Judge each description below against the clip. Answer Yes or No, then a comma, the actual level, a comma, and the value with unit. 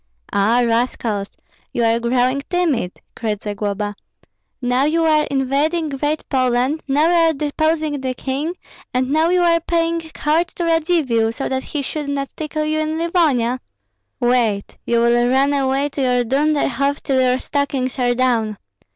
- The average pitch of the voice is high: Yes, very high, 270 Hz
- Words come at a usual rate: Yes, average, 160 wpm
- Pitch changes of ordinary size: Yes, average, 4.2 semitones